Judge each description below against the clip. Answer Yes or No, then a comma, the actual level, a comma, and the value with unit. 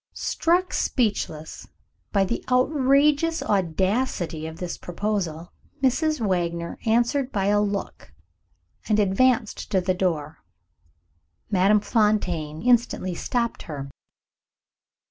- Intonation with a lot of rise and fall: Yes, wide, 6.1 semitones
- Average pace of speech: No, slow, 100 wpm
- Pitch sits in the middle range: No, high, 205 Hz